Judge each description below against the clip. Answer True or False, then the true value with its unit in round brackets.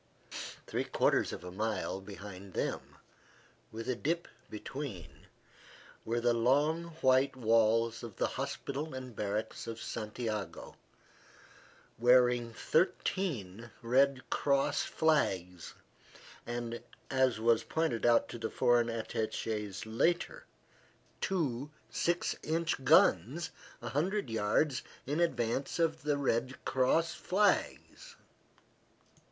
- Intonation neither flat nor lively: True (4.8 semitones)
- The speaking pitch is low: True (120 Hz)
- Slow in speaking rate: True (105 wpm)